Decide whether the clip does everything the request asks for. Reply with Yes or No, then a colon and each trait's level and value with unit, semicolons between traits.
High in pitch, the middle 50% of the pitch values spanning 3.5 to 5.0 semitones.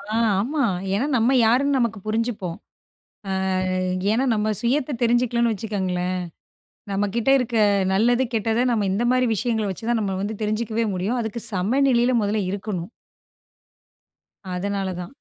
No: high, 220 Hz; average, 3.1 semitones